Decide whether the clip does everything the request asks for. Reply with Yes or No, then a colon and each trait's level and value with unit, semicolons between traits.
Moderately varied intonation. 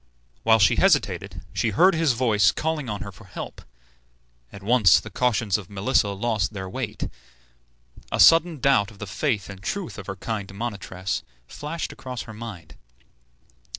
Yes: average, 4.3 semitones